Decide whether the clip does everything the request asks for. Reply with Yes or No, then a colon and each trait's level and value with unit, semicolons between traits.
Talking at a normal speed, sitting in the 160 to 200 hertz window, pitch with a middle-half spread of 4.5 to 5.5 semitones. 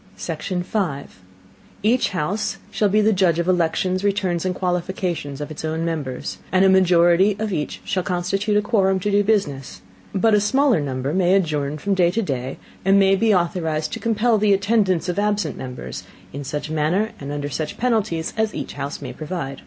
Yes: average, 190 wpm; medium, 185 Hz; average, 4.8 semitones